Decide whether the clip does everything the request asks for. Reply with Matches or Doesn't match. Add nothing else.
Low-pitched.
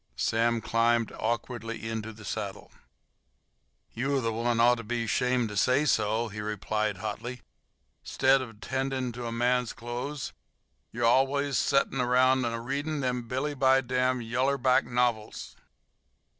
Matches